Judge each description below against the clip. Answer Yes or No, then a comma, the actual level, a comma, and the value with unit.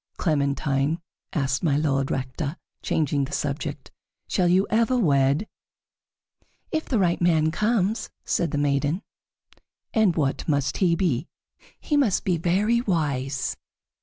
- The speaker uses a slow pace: Yes, slow, 130 wpm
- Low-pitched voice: No, medium, 160 Hz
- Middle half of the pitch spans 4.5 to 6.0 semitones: Yes, average, 5.2 semitones